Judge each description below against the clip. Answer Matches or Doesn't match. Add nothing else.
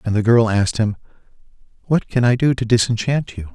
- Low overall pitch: Matches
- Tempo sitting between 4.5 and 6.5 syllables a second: Matches